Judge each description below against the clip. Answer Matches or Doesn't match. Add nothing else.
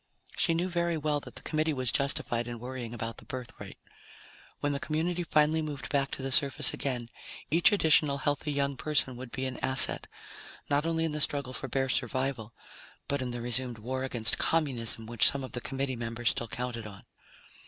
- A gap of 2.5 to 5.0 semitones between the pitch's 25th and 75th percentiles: Matches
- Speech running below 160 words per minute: Doesn't match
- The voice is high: Doesn't match